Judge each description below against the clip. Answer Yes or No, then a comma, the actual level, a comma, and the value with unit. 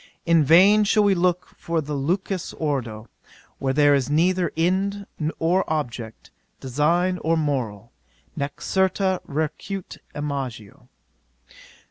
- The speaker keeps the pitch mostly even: No, average, 4.8 semitones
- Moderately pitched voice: Yes, medium, 160 Hz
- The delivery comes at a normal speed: No, slow, 115 wpm